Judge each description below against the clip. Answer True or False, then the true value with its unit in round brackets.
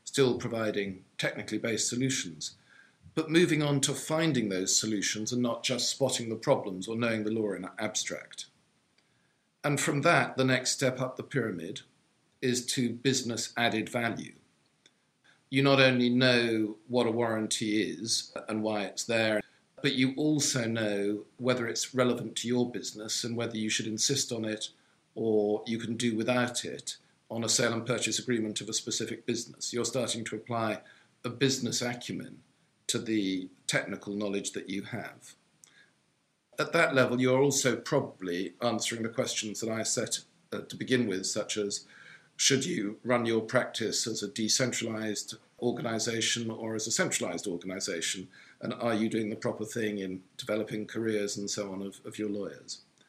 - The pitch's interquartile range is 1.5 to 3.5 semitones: True (2.5 semitones)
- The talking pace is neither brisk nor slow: True (165 wpm)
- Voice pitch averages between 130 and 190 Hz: False (115 Hz)